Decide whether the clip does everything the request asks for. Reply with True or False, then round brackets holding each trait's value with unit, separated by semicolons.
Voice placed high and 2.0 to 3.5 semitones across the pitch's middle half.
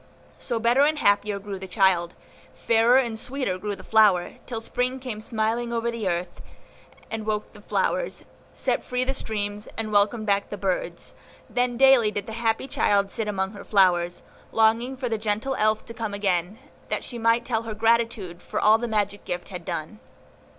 True (220 Hz; 2.7 semitones)